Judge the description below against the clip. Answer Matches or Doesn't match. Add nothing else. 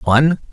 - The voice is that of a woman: Doesn't match